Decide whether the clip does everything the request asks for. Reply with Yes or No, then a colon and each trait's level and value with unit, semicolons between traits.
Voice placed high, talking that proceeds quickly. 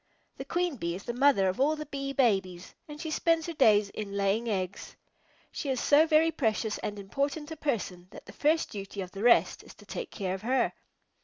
Yes: high, 240 Hz; fast, 220 wpm